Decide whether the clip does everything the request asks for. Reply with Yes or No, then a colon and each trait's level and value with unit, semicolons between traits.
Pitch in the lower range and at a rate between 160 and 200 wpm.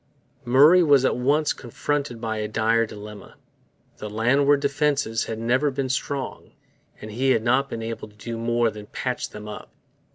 Yes: low, 120 Hz; average, 170 wpm